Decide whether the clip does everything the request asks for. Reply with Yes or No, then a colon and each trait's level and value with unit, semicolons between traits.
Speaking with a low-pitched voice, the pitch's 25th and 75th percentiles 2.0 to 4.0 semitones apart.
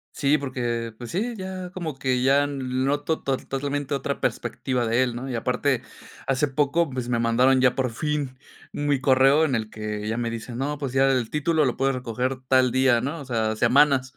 Yes: low, 130 Hz; average, 2.8 semitones